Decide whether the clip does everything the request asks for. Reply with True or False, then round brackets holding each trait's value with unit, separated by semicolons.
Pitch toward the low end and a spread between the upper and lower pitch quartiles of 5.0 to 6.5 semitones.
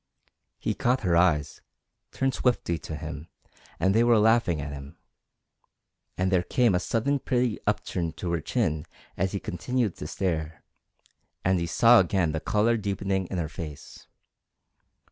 True (95 Hz; 5.3 semitones)